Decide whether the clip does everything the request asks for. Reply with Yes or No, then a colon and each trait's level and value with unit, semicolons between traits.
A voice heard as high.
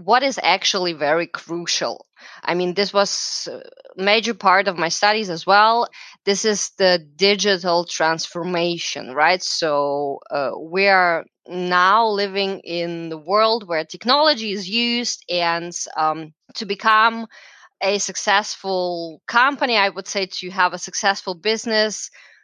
Yes: high, 195 Hz